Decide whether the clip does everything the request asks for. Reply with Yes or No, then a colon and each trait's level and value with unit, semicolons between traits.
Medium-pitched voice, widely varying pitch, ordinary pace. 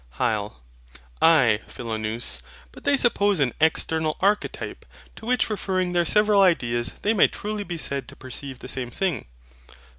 Yes: medium, 160 Hz; wide, 8.6 semitones; average, 150 wpm